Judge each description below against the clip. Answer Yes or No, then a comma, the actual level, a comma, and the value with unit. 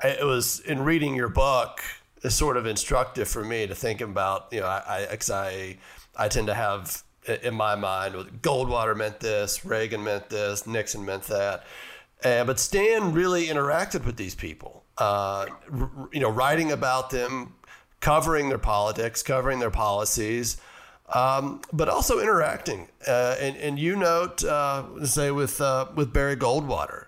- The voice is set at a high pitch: No, low, 130 Hz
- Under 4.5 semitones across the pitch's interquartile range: No, average, 5.1 semitones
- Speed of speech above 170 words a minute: No, average, 165 wpm